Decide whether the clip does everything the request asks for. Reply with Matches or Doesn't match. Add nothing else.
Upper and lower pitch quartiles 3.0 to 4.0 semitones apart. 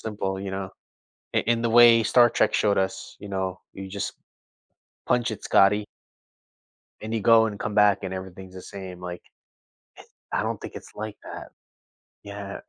Doesn't match